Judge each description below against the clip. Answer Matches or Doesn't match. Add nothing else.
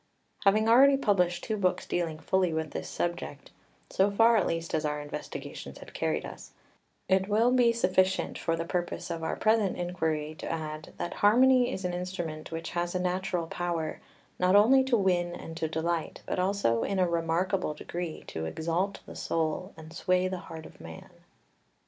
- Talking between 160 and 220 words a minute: Matches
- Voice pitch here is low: Doesn't match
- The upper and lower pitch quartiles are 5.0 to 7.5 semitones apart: Doesn't match